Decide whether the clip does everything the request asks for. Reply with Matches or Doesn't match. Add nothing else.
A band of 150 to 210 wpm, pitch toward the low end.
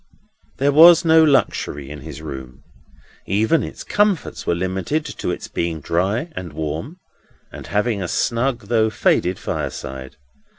Doesn't match